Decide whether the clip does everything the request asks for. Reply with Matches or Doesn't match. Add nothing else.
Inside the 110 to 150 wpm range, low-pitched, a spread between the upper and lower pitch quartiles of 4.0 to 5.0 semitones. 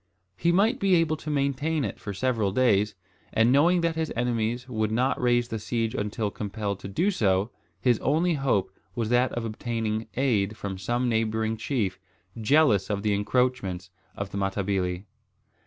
Doesn't match